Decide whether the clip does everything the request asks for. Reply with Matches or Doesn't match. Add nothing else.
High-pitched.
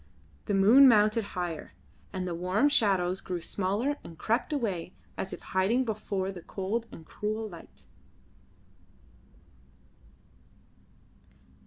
Matches